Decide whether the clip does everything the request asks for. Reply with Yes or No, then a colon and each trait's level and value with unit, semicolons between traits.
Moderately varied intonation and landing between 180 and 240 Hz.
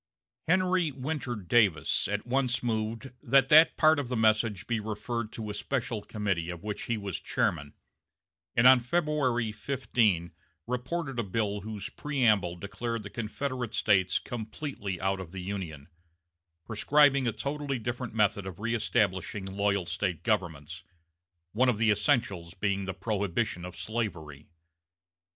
No: average, 4.3 semitones; low, 110 Hz